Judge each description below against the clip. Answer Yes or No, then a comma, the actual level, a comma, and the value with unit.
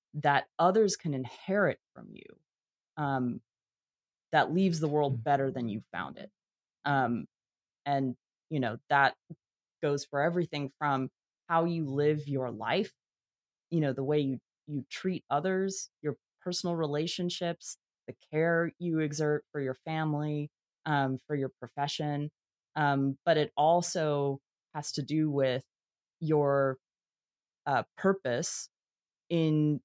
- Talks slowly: Yes, slow, 130 wpm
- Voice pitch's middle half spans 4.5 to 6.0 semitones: No, average, 3.0 semitones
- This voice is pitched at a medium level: Yes, medium, 150 Hz